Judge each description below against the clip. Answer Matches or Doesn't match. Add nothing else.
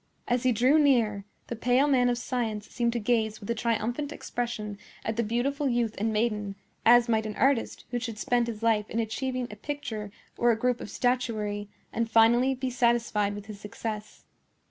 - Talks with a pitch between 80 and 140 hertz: Doesn't match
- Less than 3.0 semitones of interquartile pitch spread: Matches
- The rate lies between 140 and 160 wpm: Doesn't match